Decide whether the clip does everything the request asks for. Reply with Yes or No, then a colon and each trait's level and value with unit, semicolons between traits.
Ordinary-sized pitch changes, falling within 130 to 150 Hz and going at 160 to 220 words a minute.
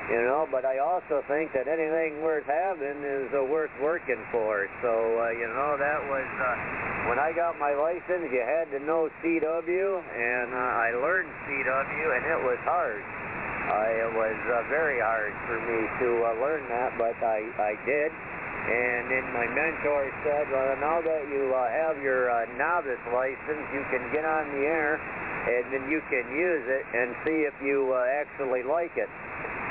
Yes: average, 4.3 semitones; medium, 140 Hz; average, 185 wpm